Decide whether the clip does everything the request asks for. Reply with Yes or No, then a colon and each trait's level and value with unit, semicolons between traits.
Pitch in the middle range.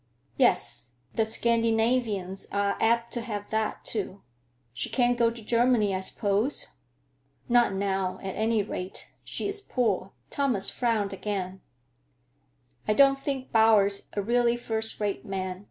No: high, 220 Hz